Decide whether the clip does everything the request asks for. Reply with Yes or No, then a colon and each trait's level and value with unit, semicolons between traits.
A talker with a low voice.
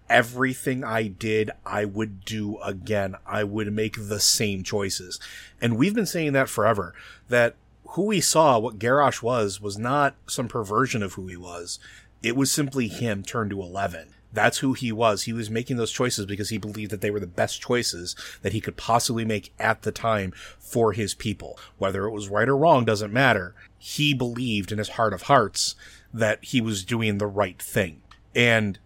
Yes: low, 110 Hz